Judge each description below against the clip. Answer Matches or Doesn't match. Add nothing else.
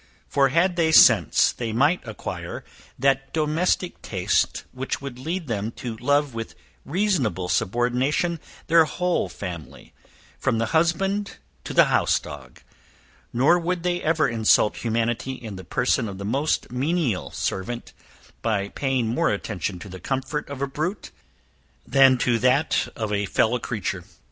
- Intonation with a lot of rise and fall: Matches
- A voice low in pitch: Matches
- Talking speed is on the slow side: Doesn't match